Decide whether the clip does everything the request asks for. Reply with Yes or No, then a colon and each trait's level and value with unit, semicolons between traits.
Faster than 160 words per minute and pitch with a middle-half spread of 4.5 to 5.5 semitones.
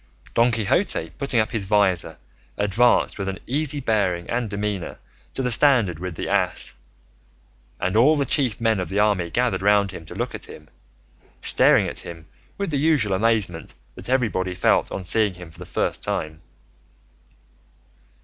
Yes: average, 170 wpm; average, 4.8 semitones